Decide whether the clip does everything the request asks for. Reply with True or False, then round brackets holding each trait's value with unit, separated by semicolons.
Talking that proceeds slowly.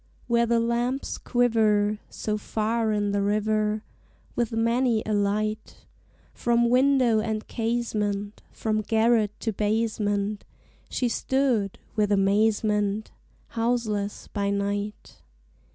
True (105 wpm)